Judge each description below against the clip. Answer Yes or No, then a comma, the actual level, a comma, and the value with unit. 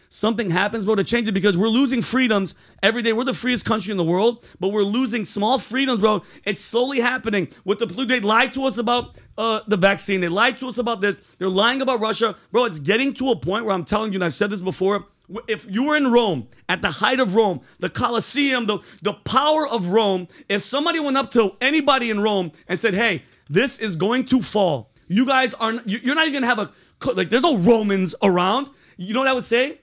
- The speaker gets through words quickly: Yes, fast, 235 wpm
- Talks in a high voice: Yes, high, 220 Hz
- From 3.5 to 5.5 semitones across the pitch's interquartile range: Yes, average, 3.8 semitones